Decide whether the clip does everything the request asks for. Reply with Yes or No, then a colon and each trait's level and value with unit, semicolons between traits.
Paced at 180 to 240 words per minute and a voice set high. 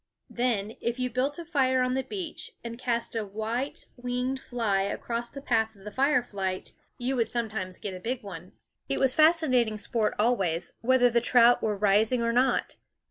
Yes: average, 185 wpm; high, 235 Hz